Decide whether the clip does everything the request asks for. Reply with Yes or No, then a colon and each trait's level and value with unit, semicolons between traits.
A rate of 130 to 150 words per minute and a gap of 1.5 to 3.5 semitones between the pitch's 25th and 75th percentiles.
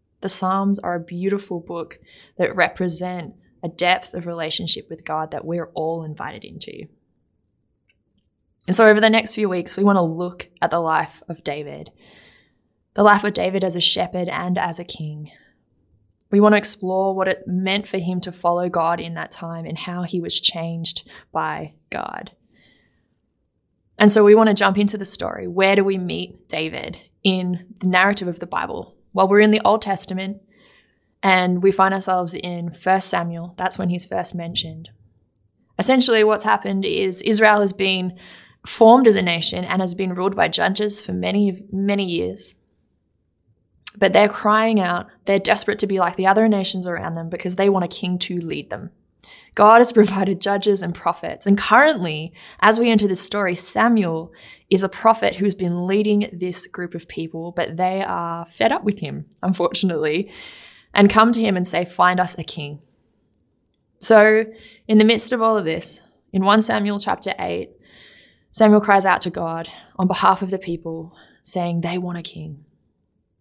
No: average, 180 wpm; average, 3.1 semitones